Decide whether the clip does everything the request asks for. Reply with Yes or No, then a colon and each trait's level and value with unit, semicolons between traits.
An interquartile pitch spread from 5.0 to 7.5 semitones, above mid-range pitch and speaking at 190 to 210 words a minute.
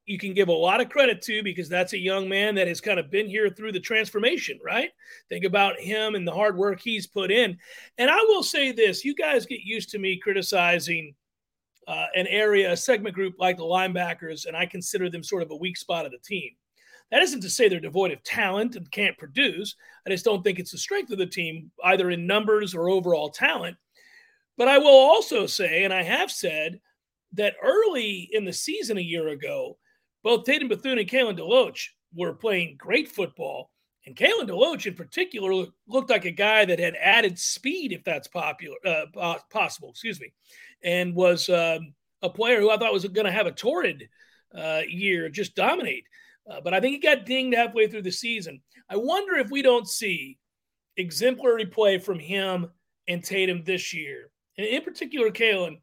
Yes: wide, 5.4 semitones; high, 205 Hz; average, 200 wpm